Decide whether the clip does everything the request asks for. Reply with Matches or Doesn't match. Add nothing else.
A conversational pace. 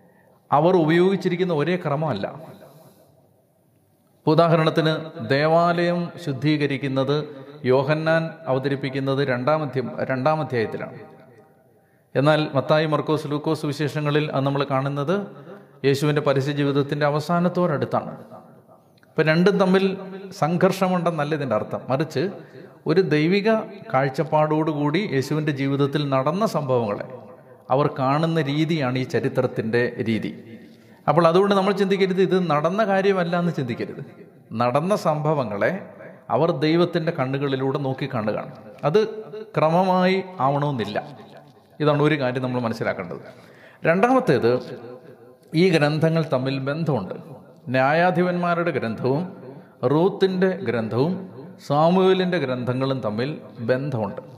Matches